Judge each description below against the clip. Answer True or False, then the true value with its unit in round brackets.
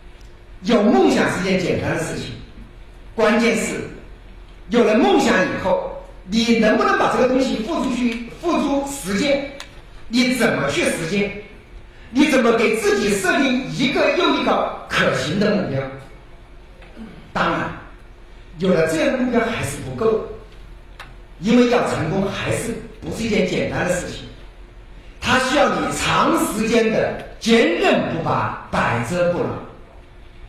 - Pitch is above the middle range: True (225 Hz)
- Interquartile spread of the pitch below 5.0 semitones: False (5.3 semitones)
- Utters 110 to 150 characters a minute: False (205 characters per minute)